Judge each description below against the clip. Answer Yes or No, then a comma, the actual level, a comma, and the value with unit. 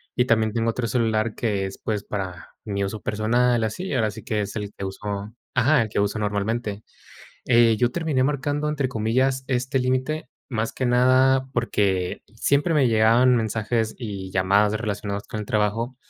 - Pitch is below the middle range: Yes, low, 115 Hz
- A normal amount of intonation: Yes, average, 3.4 semitones